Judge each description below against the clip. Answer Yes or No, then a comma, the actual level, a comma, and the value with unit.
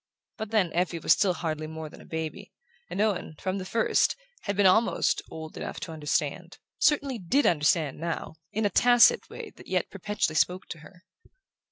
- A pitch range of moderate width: Yes, average, 4.8 semitones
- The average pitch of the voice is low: No, medium, 180 Hz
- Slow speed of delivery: No, average, 185 wpm